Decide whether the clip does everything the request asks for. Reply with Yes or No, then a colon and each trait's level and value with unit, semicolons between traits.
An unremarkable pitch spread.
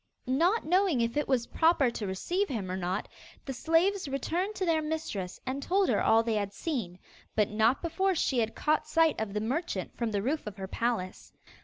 No: wide, 7.6 semitones